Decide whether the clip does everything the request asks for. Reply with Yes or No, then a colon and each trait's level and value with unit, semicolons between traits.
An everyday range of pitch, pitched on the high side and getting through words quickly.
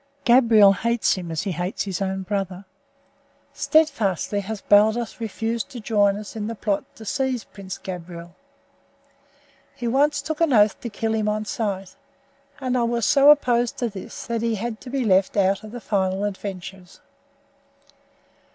No: average, 3.4 semitones; high, 215 Hz; average, 165 wpm